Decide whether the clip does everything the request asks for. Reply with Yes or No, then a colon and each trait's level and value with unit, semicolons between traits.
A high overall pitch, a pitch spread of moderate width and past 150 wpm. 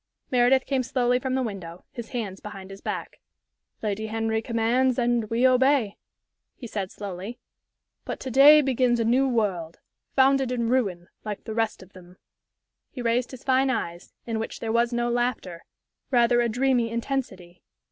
Yes: high, 235 Hz; average, 3.3 semitones; average, 170 wpm